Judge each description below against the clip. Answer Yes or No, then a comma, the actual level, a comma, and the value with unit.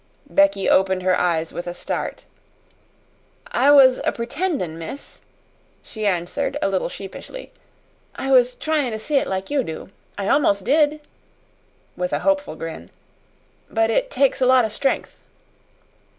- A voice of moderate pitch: No, high, 235 Hz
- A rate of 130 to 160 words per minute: Yes, average, 150 wpm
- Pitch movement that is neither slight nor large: No, wide, 7.3 semitones